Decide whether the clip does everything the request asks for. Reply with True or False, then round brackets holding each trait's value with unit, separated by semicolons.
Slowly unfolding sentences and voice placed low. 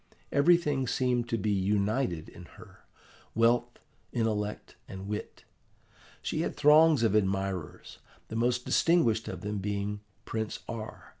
True (130 wpm; 110 Hz)